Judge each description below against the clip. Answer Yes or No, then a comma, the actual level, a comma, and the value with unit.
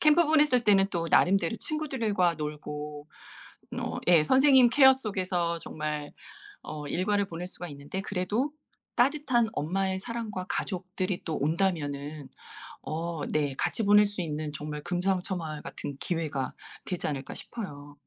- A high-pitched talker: No, medium, 180 Hz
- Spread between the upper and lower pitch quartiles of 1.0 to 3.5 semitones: No, wide, 5.6 semitones